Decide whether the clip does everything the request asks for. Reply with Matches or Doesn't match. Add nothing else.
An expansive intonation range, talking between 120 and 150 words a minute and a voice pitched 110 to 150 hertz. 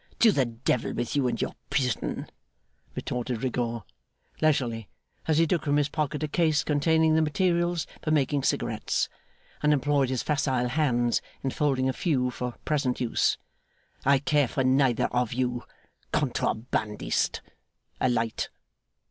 Doesn't match